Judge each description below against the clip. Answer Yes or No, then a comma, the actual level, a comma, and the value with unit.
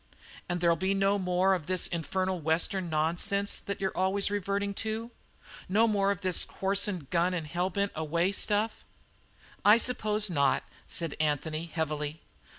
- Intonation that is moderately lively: Yes, average, 3.2 semitones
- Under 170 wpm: Yes, average, 155 wpm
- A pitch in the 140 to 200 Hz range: Yes, medium, 185 Hz